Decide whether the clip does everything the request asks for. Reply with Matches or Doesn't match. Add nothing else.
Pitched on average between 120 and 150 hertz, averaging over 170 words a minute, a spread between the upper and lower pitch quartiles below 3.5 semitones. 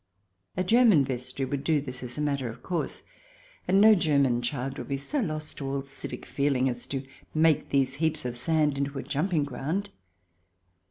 Matches